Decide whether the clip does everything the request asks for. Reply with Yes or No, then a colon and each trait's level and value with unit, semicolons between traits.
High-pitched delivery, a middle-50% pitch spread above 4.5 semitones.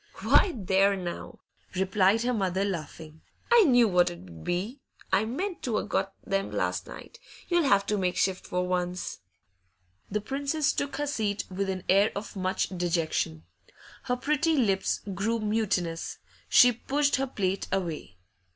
Yes: high, 195 Hz; average, 5.2 semitones